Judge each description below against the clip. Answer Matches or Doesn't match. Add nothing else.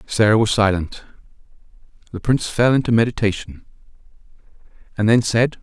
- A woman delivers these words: Doesn't match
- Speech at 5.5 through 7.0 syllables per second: Matches